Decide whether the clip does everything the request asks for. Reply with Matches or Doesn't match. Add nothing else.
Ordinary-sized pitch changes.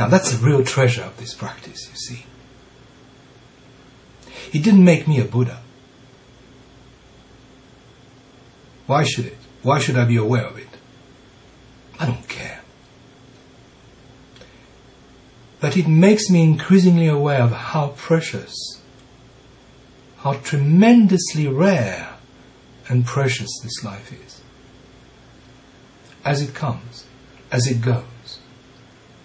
Doesn't match